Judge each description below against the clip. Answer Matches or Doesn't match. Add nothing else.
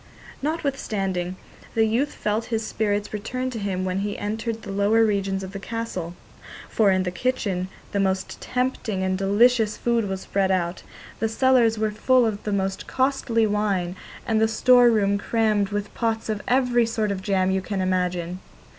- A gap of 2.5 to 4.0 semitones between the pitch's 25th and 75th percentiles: Matches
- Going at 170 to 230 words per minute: Matches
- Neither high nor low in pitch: Doesn't match